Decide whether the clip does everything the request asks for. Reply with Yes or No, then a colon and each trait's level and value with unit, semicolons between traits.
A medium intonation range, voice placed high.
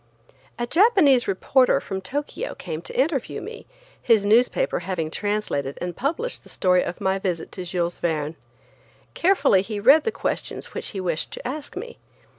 No: wide, 7.8 semitones; high, 205 Hz